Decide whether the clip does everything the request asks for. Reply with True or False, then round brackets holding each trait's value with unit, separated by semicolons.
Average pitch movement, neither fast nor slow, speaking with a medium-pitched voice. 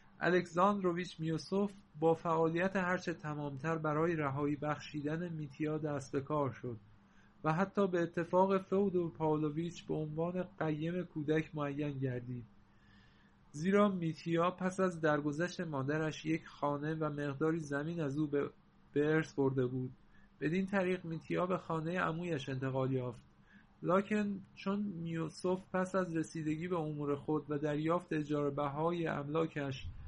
True (3.4 semitones; 130 wpm; 160 Hz)